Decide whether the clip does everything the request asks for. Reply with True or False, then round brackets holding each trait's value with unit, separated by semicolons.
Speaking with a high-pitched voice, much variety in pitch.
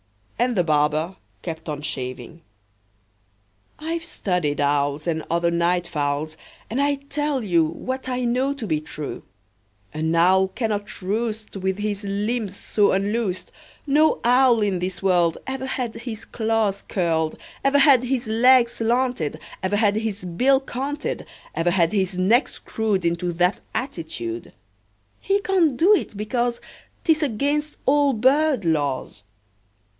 True (210 Hz; 7.1 semitones)